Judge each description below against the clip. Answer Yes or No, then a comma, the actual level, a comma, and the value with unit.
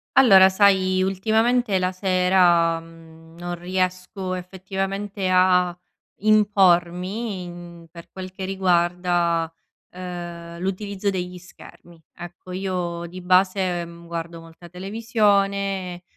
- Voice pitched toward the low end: No, medium, 185 Hz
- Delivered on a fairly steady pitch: Yes, narrow, 1.8 semitones